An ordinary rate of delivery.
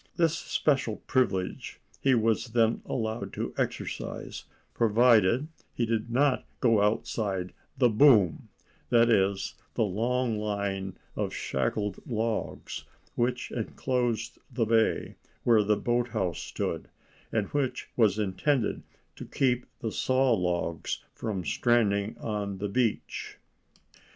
No: slow, 115 wpm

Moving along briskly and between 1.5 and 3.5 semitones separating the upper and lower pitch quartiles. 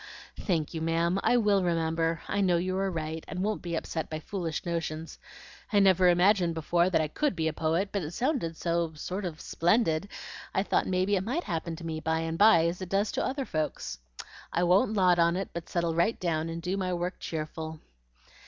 Yes: fast, 220 wpm; average, 2.8 semitones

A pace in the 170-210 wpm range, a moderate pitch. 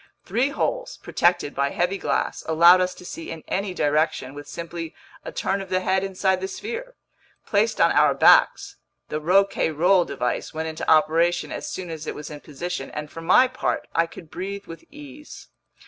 Yes: average, 185 wpm; medium, 175 Hz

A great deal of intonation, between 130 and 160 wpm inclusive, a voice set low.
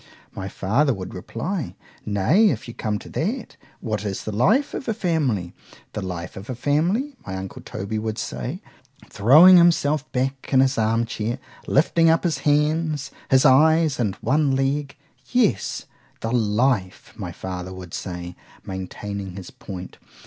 Yes: wide, 7.6 semitones; average, 140 wpm; low, 125 Hz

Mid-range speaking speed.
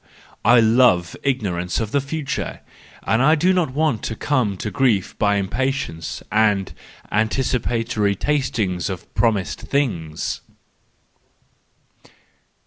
No: slow, 110 wpm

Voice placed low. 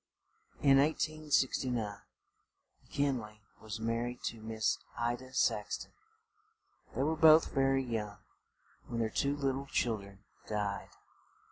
Yes: low, 120 Hz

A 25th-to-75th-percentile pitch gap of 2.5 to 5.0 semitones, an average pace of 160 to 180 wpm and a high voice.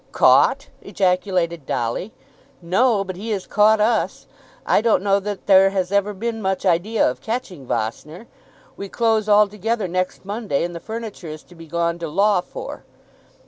Yes: average, 3.7 semitones; average, 165 wpm; high, 195 Hz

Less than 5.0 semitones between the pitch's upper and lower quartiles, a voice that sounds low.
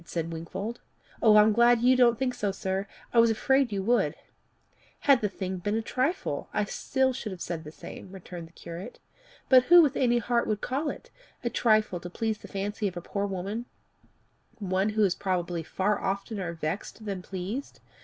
No: average, 4.3 semitones; high, 205 Hz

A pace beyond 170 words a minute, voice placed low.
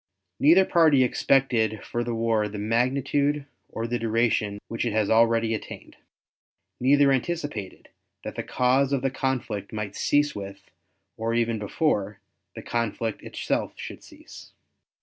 No: average, 140 wpm; low, 115 Hz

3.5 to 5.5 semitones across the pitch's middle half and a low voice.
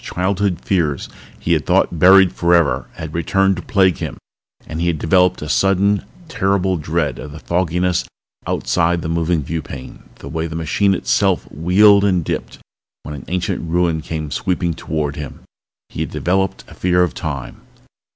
No: average, 2.9 semitones; very low, 85 Hz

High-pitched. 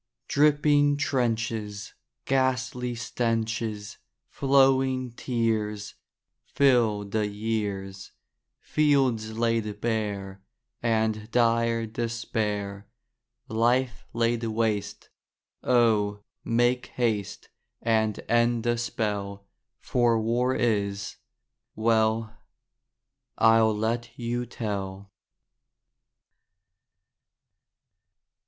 No: low, 115 Hz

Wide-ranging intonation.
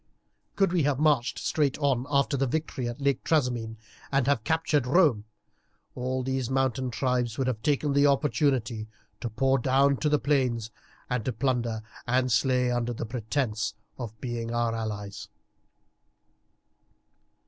No: average, 3.1 semitones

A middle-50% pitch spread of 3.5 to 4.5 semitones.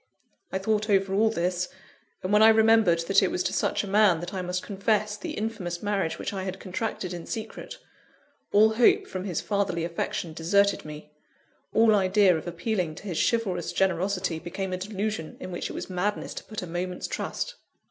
No: average, 3.0 semitones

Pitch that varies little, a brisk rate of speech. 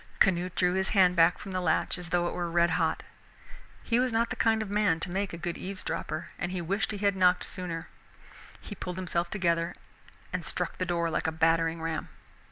Yes: narrow, 2.3 semitones; fast, 215 wpm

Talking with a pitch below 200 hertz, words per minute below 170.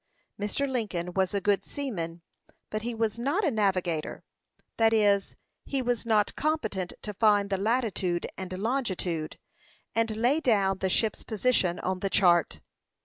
No: high, 205 Hz; average, 150 wpm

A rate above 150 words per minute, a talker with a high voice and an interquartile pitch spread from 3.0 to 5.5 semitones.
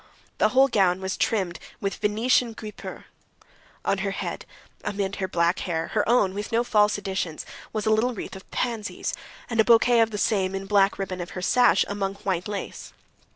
No: average, 185 wpm; high, 205 Hz; narrow, 2.6 semitones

